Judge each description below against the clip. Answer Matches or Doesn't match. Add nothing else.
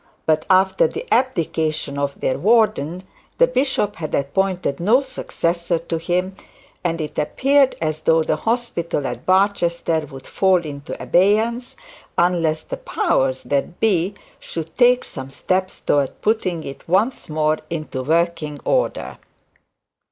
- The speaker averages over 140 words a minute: Doesn't match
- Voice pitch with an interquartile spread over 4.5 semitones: Matches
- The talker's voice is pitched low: Doesn't match